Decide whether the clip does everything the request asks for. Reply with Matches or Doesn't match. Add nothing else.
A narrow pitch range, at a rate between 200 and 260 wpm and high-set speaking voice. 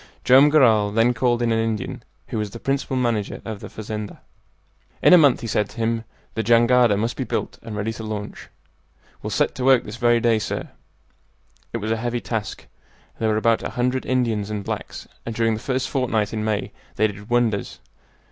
Doesn't match